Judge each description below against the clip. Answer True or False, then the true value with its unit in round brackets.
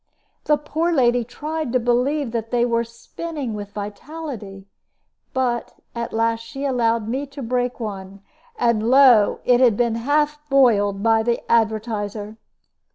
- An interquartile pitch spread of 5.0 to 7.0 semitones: False (3.3 semitones)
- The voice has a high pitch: True (235 Hz)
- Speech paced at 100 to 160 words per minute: True (145 wpm)